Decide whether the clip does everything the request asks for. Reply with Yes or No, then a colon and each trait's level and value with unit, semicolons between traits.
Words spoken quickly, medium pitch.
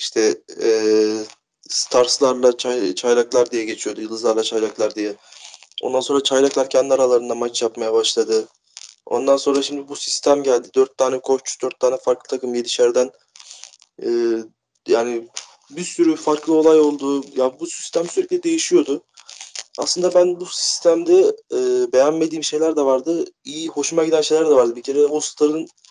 Yes: fast, 145 wpm; medium, 150 Hz